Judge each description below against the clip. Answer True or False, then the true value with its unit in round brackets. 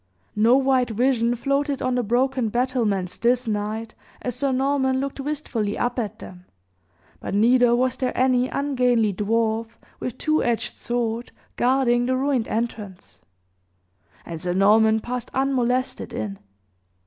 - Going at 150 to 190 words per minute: False (135 wpm)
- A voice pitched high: True (245 Hz)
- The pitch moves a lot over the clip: False (2.9 semitones)